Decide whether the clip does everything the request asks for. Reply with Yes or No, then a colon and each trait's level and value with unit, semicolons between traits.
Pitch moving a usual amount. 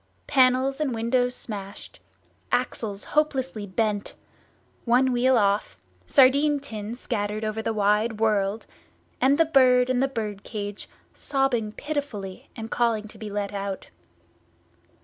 Yes: average, 3.9 semitones